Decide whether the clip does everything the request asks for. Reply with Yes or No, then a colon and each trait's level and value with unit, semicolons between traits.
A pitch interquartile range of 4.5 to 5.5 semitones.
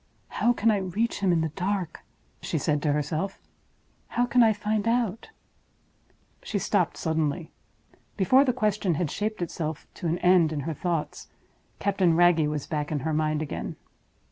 Yes: average, 5.1 semitones